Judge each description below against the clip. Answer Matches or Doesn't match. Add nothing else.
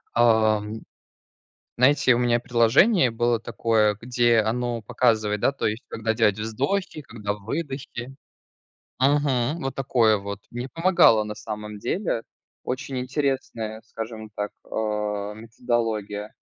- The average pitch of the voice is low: Matches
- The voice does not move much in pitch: Doesn't match